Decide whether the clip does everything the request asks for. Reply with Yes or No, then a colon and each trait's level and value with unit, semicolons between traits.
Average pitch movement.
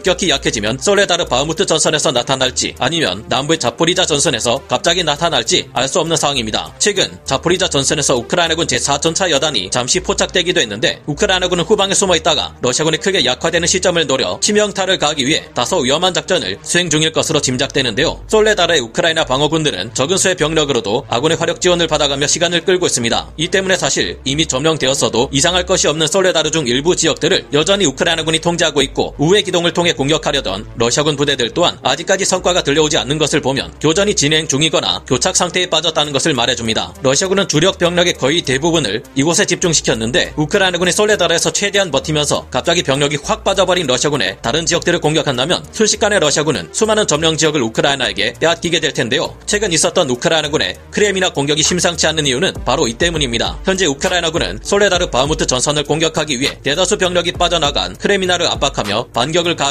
Yes: average, 4.1 semitones